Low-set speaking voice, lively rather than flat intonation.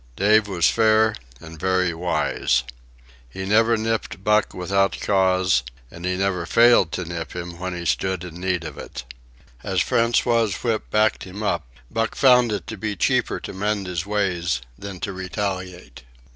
No: very low, 95 Hz; average, 3.4 semitones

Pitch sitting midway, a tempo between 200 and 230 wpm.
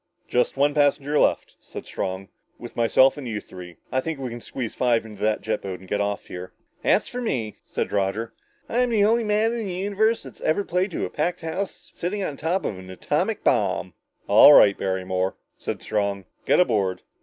No: low, 125 Hz; fast, 205 wpm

